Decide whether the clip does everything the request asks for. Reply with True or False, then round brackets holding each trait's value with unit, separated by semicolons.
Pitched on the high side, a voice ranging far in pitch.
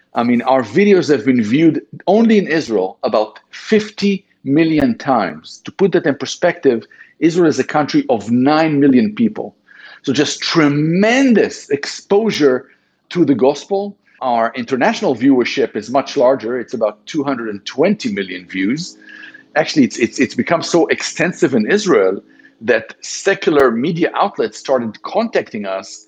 False (175 Hz; 8.0 semitones)